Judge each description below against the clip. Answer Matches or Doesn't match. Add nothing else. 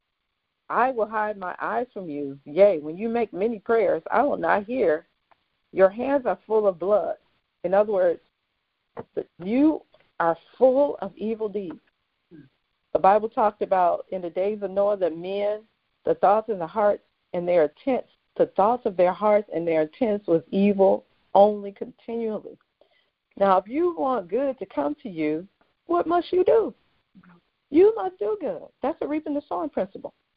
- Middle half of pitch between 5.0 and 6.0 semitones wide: Matches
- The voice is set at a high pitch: Matches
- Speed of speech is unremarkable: Matches